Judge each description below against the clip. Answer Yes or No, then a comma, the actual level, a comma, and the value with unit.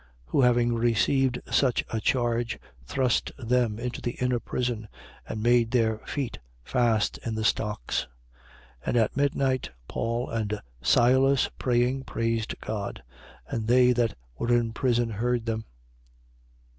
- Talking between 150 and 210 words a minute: No, average, 140 wpm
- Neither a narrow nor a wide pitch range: No, narrow, 1.9 semitones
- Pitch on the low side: Yes, low, 120 Hz